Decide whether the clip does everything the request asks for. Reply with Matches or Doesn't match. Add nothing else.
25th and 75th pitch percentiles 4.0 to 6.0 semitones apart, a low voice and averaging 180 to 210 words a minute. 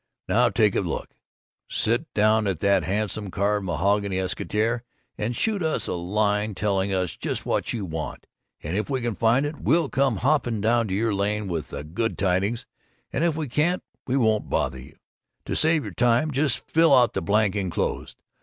Matches